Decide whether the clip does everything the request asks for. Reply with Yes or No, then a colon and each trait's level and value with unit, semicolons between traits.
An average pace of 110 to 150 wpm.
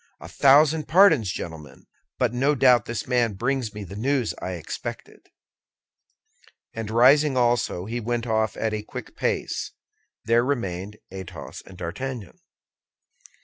Yes: slow, 135 wpm